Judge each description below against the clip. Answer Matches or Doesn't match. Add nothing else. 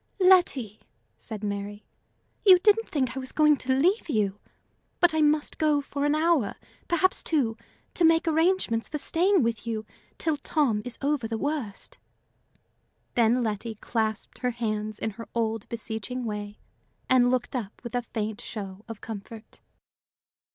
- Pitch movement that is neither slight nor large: Doesn't match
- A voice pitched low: Doesn't match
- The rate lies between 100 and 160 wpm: Matches